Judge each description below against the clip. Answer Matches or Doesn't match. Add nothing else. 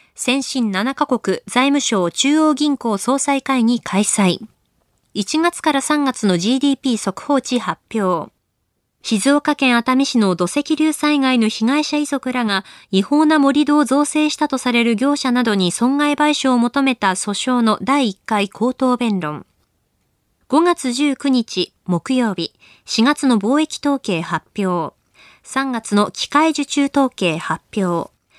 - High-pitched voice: Matches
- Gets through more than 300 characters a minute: Doesn't match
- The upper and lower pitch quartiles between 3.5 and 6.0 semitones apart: Matches